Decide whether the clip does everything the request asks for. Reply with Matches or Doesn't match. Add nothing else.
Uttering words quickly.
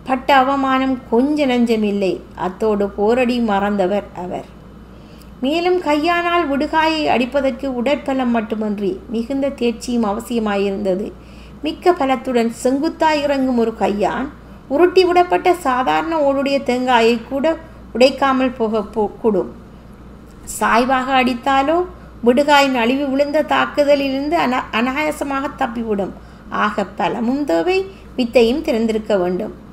Doesn't match